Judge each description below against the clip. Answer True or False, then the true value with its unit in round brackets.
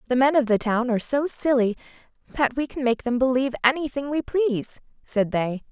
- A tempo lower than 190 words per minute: False (200 wpm)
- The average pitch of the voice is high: True (255 Hz)